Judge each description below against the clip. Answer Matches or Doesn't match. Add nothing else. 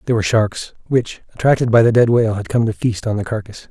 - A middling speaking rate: Doesn't match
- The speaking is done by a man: Matches